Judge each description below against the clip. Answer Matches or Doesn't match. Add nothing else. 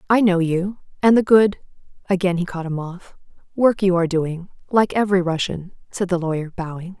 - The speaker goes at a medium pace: Matches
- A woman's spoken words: Matches